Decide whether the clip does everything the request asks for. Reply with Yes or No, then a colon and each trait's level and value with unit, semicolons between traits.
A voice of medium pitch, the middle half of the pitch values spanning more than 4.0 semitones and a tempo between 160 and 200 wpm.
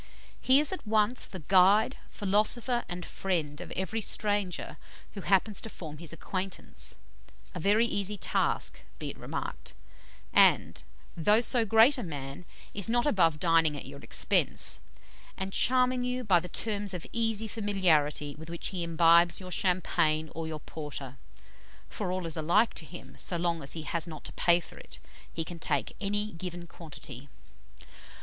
Yes: medium, 180 Hz; average, 4.4 semitones; average, 165 wpm